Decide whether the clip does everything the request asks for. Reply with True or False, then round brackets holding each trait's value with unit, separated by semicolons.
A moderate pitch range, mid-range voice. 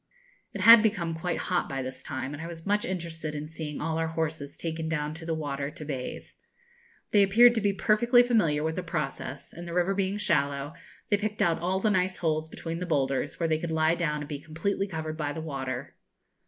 True (3.8 semitones; 165 Hz)